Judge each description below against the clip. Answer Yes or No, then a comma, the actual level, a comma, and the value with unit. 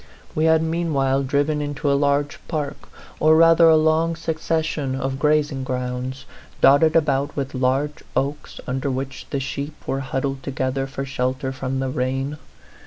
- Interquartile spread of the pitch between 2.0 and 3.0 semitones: Yes, narrow, 2.4 semitones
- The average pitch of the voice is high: No, medium, 140 Hz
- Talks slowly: No, average, 155 wpm